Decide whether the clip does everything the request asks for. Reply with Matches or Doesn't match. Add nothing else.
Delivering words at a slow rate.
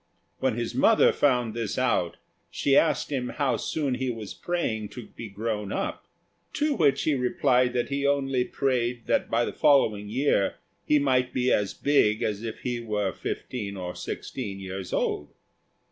Doesn't match